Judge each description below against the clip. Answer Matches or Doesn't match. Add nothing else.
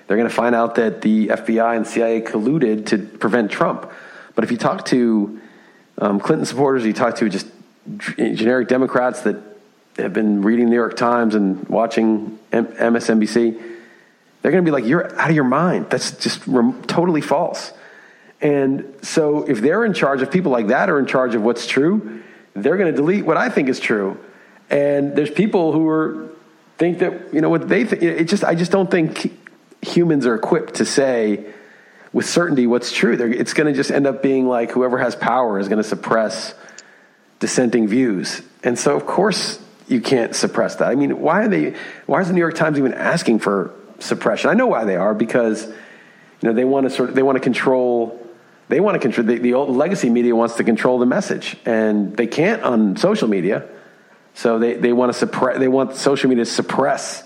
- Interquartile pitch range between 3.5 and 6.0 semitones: Matches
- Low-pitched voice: Matches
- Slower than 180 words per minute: Doesn't match